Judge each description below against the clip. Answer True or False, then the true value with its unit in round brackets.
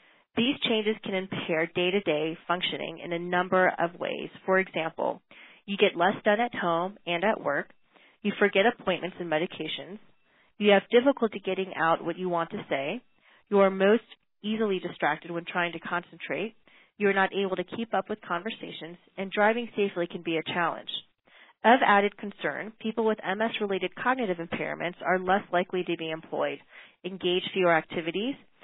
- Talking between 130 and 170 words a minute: True (165 wpm)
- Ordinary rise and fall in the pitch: True (3.3 semitones)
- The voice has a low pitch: False (190 Hz)